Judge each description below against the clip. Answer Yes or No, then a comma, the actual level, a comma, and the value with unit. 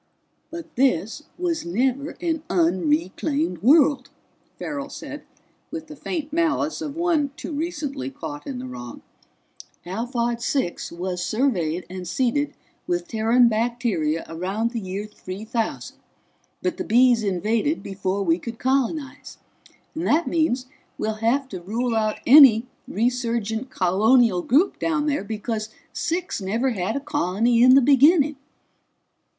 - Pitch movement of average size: No, wide, 7.0 semitones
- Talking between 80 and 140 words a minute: Yes, slow, 135 wpm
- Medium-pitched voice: No, high, 235 Hz